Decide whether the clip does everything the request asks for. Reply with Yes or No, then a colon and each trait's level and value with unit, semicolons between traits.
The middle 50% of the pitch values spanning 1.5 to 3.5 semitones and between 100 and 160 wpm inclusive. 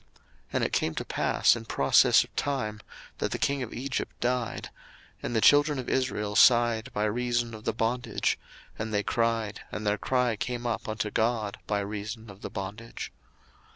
No: narrow, 2.6 semitones; average, 185 wpm